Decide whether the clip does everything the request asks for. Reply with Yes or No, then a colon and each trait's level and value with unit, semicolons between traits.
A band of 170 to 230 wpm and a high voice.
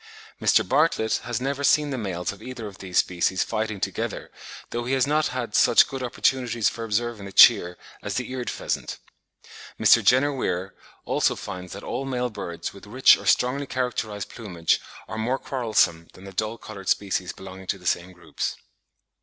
No: average, 180 wpm; low, 110 Hz